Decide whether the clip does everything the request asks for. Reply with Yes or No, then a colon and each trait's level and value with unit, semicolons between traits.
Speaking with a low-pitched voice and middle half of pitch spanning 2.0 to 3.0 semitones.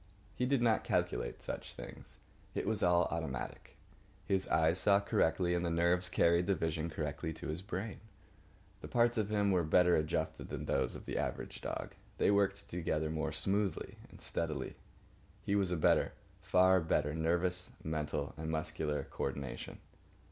No: very low, 85 Hz; average, 3.5 semitones